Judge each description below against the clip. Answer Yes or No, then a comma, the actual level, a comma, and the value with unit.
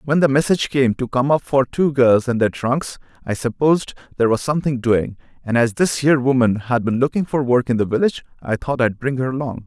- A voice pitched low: Yes, low, 130 Hz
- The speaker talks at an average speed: No, fast, 235 wpm